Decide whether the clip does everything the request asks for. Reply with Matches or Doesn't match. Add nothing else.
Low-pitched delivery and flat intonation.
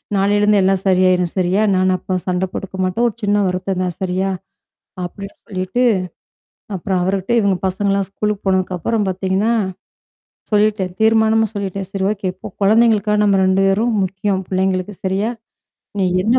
Doesn't match